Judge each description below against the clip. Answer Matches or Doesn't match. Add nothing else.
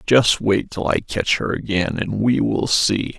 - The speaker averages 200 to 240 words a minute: Matches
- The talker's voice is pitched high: Doesn't match